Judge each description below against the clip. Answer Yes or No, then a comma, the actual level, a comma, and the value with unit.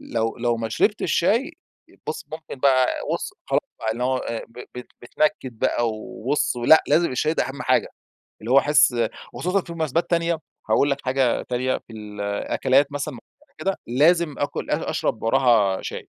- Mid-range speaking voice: No, low, 130 Hz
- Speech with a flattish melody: No, average, 4.9 semitones